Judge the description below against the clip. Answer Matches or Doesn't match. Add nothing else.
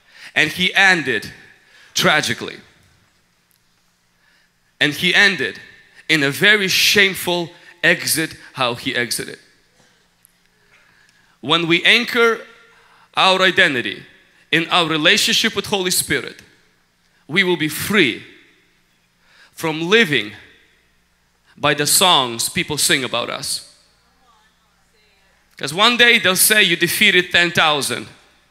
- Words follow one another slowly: Matches